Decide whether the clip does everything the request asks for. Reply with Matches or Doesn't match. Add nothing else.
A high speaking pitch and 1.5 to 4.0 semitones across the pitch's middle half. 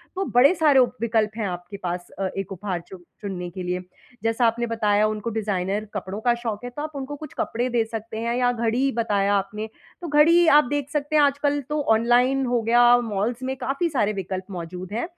Doesn't match